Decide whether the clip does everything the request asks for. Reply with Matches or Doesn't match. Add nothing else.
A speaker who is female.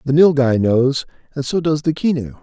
Doesn't match